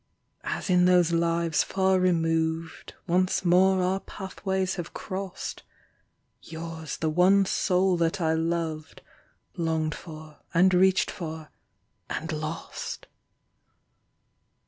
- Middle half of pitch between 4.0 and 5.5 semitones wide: No, narrow, 2.4 semitones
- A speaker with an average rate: No, slow, 105 wpm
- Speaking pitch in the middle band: Yes, medium, 170 Hz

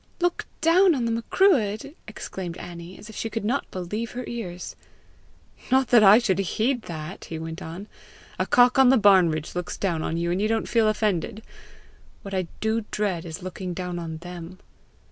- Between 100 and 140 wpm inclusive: No, average, 190 wpm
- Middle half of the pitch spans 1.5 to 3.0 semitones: No, average, 4.7 semitones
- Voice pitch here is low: No, high, 200 Hz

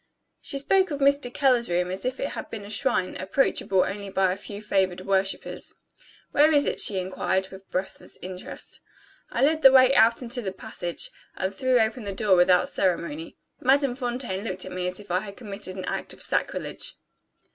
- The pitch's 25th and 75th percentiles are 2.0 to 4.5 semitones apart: No, average, 5.3 semitones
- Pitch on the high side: Yes, high, 200 Hz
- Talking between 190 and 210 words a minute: Yes, average, 195 wpm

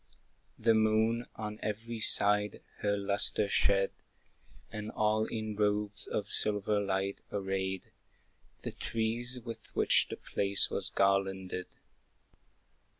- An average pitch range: No, narrow, 1.9 semitones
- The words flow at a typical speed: No, slow, 110 wpm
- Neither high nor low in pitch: No, low, 105 Hz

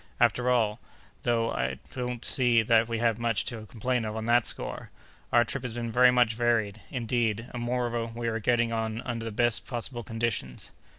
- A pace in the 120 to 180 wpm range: No, average, 190 wpm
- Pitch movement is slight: Yes, narrow, 1.3 semitones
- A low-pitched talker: Yes, low, 115 Hz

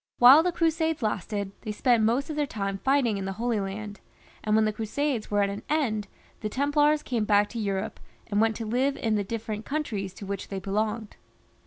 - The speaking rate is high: Yes, fast, 210 wpm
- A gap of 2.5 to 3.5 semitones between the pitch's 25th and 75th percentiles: No, average, 4.6 semitones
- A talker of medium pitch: No, high, 220 Hz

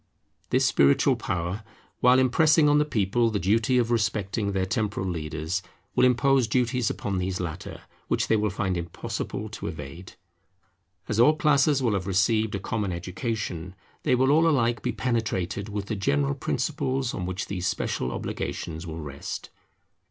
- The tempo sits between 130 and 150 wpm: No, average, 160 wpm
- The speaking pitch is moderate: No, low, 105 Hz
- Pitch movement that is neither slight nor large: Yes, average, 4.9 semitones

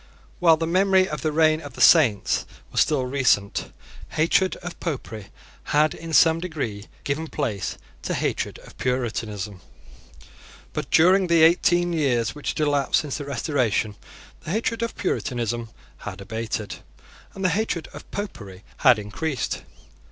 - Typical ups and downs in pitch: No, wide, 6.5 semitones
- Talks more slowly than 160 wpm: Yes, average, 145 wpm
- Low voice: No, medium, 150 Hz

